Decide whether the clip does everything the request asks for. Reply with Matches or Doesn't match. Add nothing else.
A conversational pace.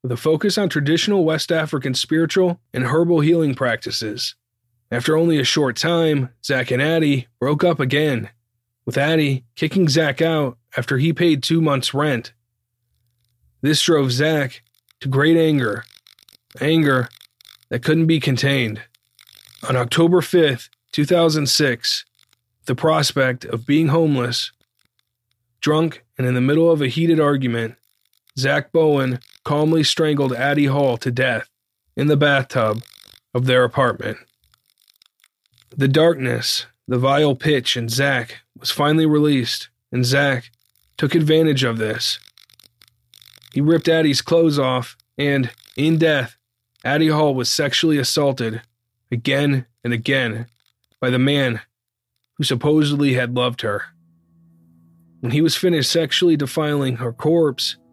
Doesn't match